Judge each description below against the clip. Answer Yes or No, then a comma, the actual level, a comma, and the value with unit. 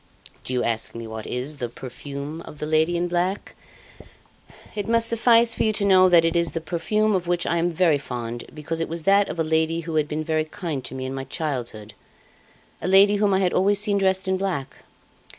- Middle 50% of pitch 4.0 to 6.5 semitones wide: Yes, average, 4.9 semitones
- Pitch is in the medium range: Yes, medium, 165 Hz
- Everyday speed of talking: No, fast, 225 wpm